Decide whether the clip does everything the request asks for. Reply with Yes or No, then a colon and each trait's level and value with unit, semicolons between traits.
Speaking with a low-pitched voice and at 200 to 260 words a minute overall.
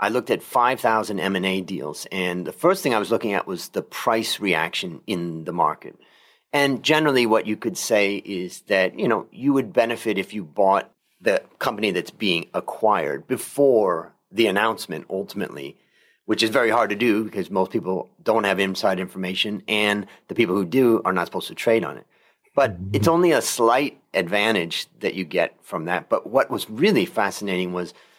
No: low, 100 Hz; average, 185 wpm